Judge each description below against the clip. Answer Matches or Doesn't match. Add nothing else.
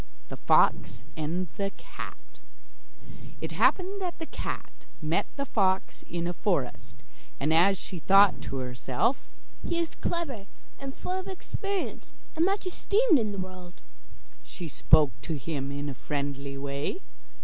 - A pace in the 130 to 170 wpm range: Matches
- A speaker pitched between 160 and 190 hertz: Matches